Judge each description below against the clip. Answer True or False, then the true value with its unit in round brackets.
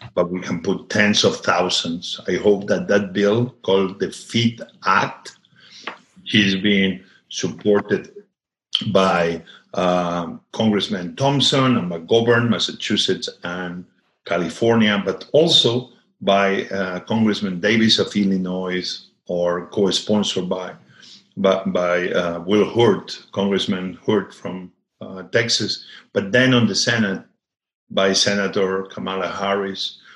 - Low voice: True (95 Hz)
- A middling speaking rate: False (115 wpm)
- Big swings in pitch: False (2.9 semitones)